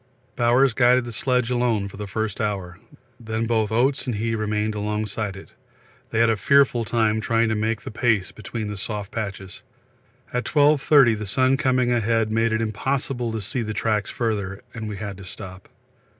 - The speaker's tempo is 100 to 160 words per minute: No, average, 185 wpm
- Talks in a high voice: No, low, 110 Hz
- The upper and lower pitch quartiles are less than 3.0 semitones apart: Yes, narrow, 2.5 semitones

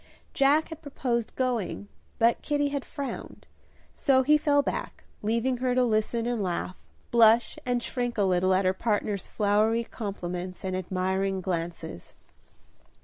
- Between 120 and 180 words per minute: Yes, average, 145 wpm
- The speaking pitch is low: No, high, 225 Hz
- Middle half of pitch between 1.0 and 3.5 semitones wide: No, average, 5.1 semitones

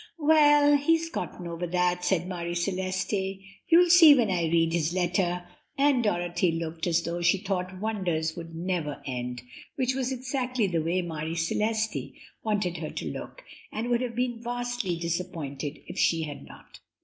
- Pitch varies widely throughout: Yes, wide, 6.2 semitones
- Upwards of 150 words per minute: Yes, average, 165 wpm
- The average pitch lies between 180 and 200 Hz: Yes, medium, 185 Hz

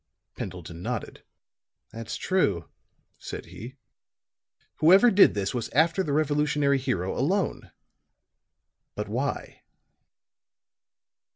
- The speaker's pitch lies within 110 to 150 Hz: Yes, medium, 140 Hz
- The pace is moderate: No, slow, 90 wpm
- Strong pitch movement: Yes, wide, 7.7 semitones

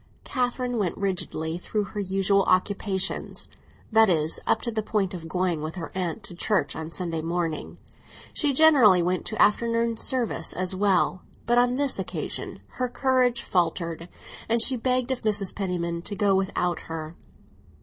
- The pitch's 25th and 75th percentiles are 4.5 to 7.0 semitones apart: Yes, average, 5.0 semitones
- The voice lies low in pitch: No, high, 195 Hz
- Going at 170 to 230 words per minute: No, average, 160 wpm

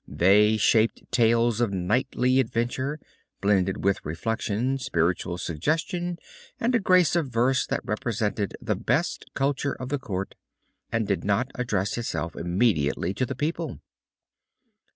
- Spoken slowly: Yes, slow, 130 wpm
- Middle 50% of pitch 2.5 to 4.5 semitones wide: No, average, 5.2 semitones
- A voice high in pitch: No, low, 115 Hz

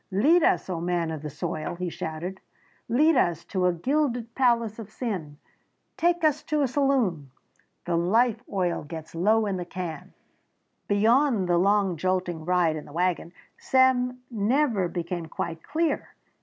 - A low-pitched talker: No, high, 190 Hz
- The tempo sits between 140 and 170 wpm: Yes, average, 155 wpm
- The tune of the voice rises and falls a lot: Yes, wide, 6.4 semitones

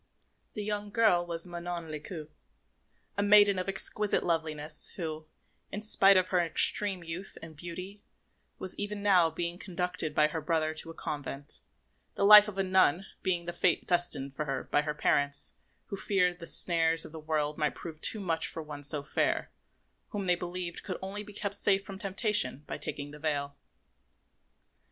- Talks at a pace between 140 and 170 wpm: No, average, 180 wpm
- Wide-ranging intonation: No, average, 3.9 semitones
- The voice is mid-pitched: Yes, medium, 175 Hz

